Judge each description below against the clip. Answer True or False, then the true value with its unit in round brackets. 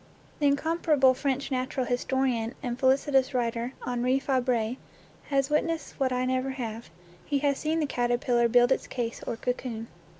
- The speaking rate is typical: True (155 wpm)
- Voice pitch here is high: True (255 Hz)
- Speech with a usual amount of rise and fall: False (2.1 semitones)